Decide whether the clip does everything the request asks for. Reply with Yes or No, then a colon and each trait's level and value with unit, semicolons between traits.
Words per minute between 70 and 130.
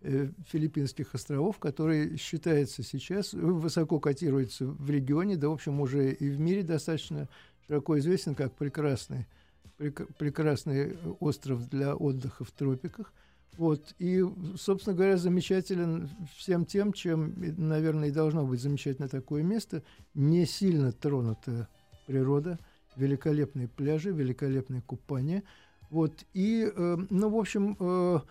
Yes: average, 125 wpm